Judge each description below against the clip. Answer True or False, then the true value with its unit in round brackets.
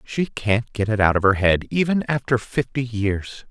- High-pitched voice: False (115 Hz)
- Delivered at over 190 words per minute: True (205 wpm)